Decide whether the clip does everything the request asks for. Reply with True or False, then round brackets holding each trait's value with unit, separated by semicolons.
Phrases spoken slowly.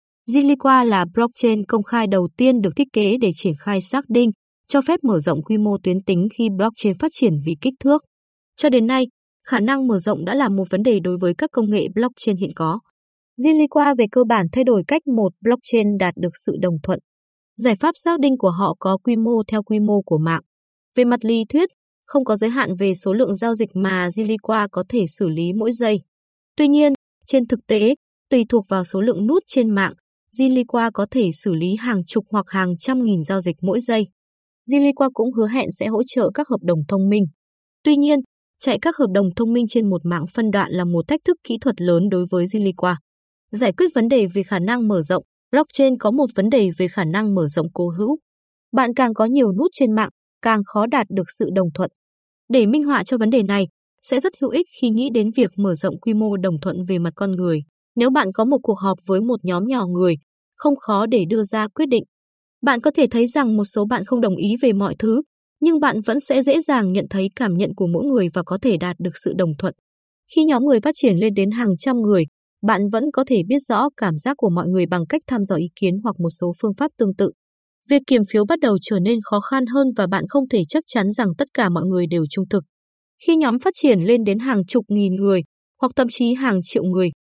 False (240 wpm)